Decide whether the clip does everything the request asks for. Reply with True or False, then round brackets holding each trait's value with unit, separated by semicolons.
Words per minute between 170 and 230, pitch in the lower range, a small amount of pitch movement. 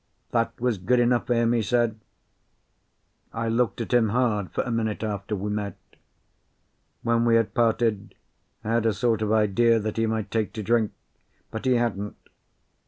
True (175 wpm; 115 Hz; 1.8 semitones)